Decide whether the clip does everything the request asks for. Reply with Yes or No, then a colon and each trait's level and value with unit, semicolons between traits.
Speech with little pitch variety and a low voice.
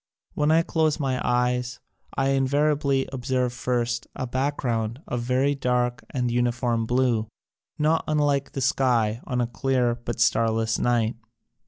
Yes: narrow, 2.3 semitones; low, 125 Hz